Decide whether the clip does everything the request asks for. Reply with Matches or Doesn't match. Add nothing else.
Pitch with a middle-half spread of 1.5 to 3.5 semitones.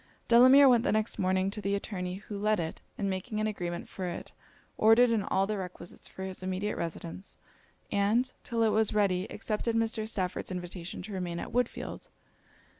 Matches